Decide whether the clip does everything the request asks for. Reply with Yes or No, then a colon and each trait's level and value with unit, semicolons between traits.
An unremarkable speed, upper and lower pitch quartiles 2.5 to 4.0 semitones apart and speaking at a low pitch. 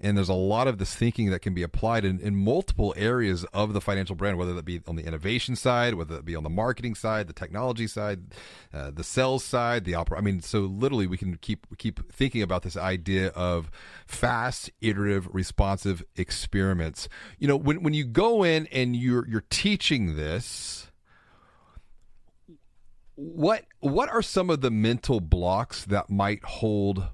No: average, 180 wpm; average, 4.7 semitones; low, 100 Hz